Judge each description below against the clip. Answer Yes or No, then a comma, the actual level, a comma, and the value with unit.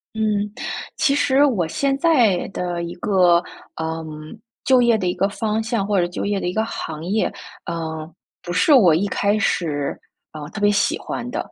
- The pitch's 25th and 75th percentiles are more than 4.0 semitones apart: Yes, average, 4.5 semitones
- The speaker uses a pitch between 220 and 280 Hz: No, high, 200 Hz